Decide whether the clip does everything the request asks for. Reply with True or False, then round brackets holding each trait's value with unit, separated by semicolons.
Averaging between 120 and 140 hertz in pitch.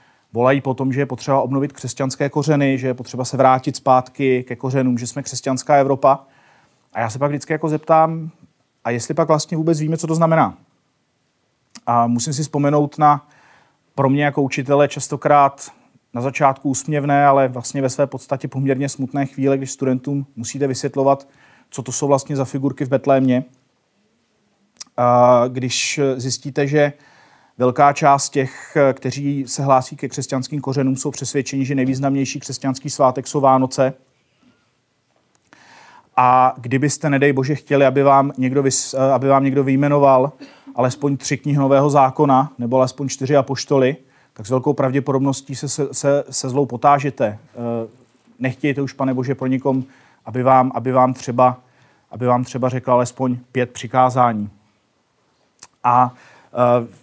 True (135 Hz)